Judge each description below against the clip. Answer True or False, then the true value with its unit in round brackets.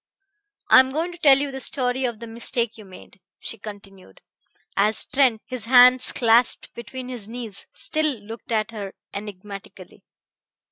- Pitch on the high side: True (235 Hz)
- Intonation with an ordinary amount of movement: True (3.6 semitones)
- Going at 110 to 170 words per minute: True (155 wpm)